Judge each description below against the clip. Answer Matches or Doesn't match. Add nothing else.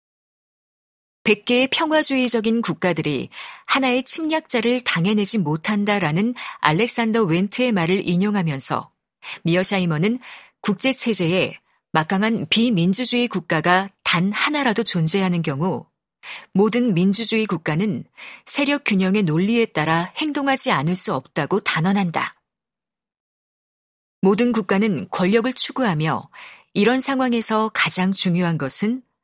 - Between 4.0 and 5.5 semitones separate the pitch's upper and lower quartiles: Matches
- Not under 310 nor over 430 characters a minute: Doesn't match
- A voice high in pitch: Matches